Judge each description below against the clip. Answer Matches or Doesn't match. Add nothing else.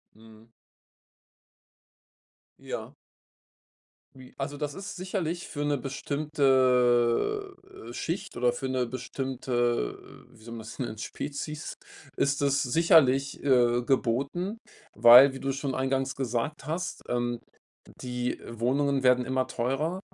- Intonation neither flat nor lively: Matches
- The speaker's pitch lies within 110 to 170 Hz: Matches